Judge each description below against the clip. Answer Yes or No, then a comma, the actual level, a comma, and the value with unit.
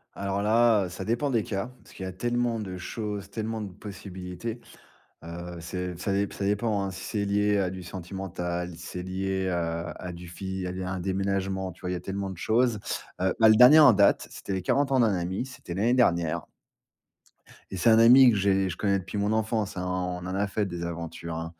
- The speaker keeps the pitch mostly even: No, average, 3.0 semitones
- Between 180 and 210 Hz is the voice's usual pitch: No, very low, 95 Hz